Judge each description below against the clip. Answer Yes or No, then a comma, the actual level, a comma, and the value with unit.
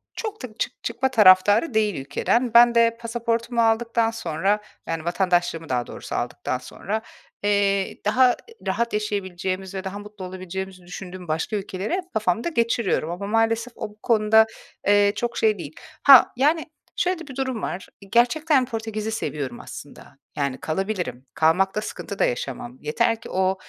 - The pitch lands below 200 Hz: No, high, 210 Hz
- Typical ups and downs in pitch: Yes, average, 4.0 semitones